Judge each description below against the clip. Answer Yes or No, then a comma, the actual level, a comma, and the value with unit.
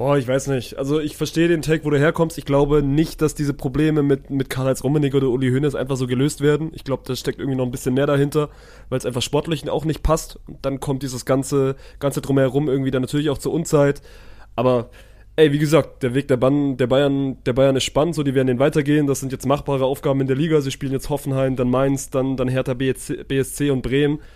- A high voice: No, medium, 140 Hz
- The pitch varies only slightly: Yes, narrow, 2.0 semitones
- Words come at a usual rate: No, fast, 245 wpm